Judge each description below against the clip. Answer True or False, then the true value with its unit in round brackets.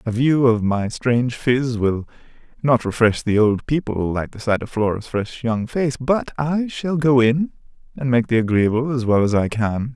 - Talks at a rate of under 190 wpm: False (205 wpm)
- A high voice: False (120 Hz)